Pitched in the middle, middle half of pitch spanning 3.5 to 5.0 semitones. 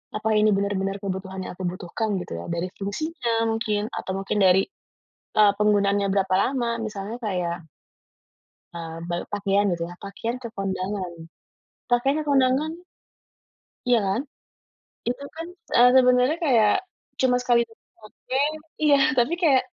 No: high, 210 Hz; average, 4.4 semitones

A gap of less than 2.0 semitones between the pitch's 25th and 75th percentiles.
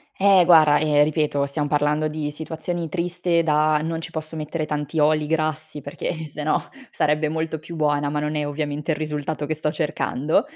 Yes: narrow, 1.2 semitones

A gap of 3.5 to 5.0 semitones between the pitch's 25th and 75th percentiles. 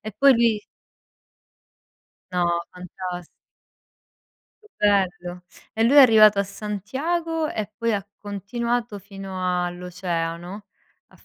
Yes: average, 4.3 semitones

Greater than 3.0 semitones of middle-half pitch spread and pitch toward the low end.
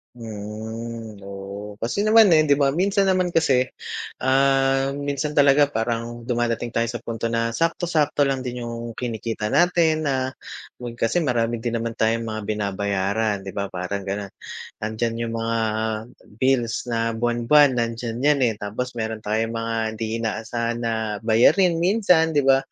Yes: average, 3.7 semitones; low, 115 Hz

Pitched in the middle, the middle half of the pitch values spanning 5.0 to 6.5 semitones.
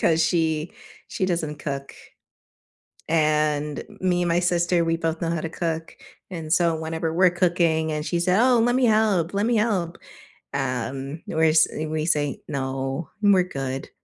No: medium, 165 Hz; average, 2.7 semitones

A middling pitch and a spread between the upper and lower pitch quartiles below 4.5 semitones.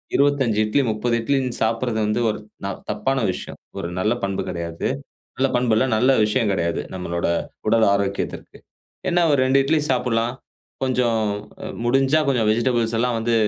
No: low, 115 Hz; average, 3.4 semitones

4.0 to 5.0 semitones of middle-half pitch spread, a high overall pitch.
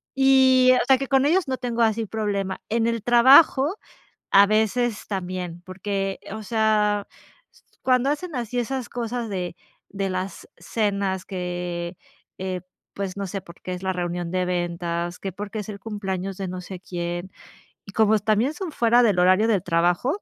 Yes: average, 4.5 semitones; high, 200 Hz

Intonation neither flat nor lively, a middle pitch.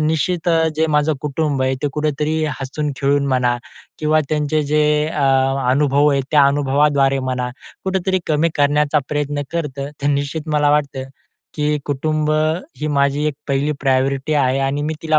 No: narrow, 1.8 semitones; medium, 145 Hz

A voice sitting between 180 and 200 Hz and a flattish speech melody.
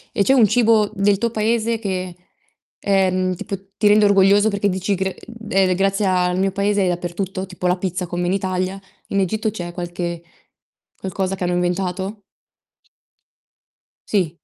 Yes: high, 190 Hz; narrow, 2.1 semitones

